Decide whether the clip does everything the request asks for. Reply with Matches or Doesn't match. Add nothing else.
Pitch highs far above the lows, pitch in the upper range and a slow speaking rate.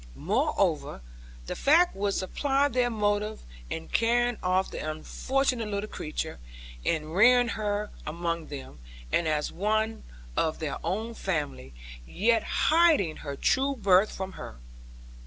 Matches